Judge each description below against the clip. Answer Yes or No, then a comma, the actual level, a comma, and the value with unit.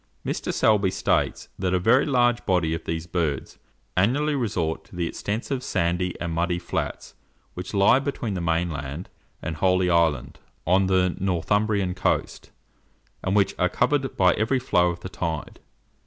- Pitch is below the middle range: Yes, very low, 90 Hz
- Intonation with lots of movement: No, average, 3.7 semitones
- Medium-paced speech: Yes, average, 155 wpm